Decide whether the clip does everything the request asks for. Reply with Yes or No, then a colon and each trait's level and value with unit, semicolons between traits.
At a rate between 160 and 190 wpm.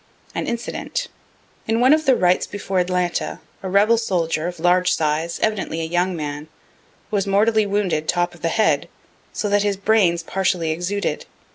Yes: average, 165 wpm